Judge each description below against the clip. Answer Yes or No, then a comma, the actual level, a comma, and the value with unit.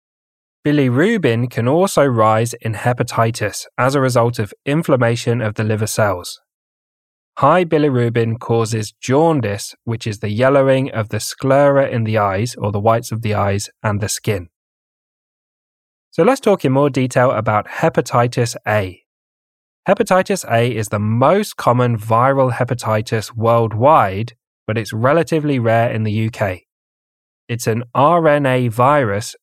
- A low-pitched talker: Yes, low, 115 Hz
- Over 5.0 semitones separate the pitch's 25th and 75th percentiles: No, average, 3.7 semitones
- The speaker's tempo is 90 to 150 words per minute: Yes, slow, 135 wpm